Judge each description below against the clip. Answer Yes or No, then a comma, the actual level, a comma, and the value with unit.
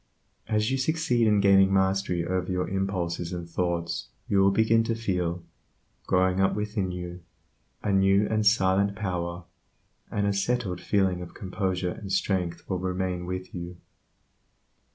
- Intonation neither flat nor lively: No, narrow, 2.2 semitones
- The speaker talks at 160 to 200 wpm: No, average, 150 wpm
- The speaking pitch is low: Yes, very low, 95 Hz